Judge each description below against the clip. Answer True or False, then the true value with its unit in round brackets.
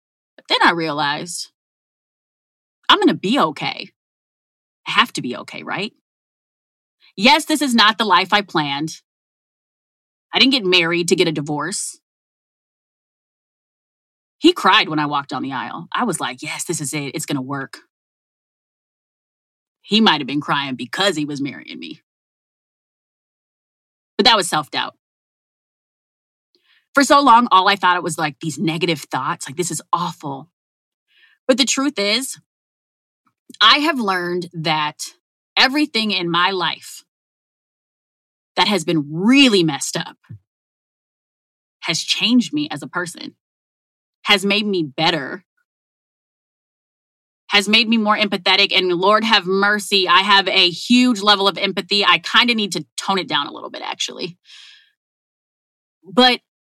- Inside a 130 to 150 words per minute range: True (145 wpm)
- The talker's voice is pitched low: False (185 Hz)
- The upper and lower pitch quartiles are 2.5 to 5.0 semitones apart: False (5.5 semitones)